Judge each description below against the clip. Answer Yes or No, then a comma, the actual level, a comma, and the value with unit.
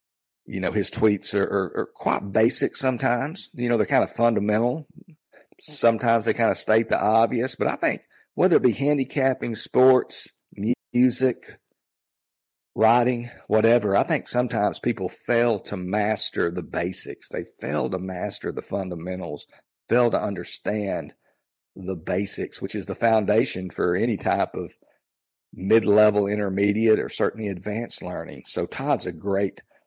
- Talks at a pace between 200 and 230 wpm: No, average, 145 wpm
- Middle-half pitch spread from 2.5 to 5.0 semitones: Yes, average, 3.7 semitones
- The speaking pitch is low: Yes, low, 110 Hz